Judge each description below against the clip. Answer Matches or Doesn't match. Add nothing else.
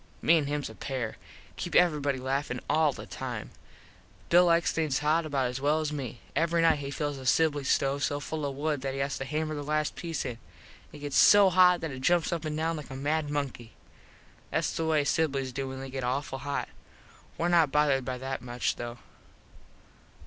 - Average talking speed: Doesn't match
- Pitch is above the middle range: Doesn't match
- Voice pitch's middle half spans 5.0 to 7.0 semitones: Doesn't match